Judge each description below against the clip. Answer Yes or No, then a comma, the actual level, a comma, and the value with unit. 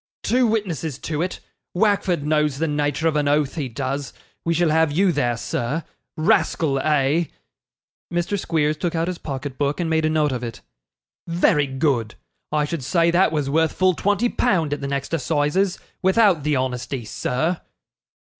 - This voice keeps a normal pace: Yes, average, 170 wpm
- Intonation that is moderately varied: Yes, average, 3.5 semitones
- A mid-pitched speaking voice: Yes, medium, 155 Hz